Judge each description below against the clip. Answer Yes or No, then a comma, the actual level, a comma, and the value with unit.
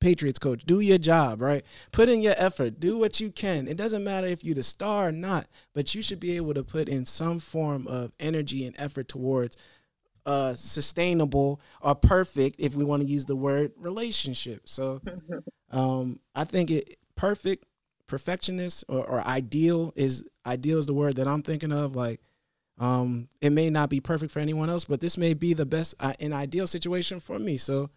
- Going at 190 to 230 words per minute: Yes, average, 200 wpm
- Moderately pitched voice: Yes, medium, 150 Hz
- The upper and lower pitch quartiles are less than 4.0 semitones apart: No, average, 4.5 semitones